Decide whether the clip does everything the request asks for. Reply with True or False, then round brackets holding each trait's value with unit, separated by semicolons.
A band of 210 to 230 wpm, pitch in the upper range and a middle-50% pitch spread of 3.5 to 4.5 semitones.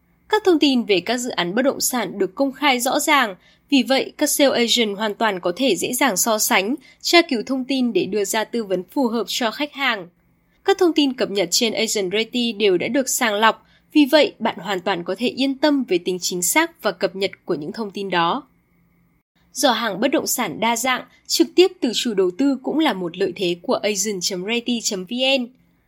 False (220 wpm; 235 Hz; 5.4 semitones)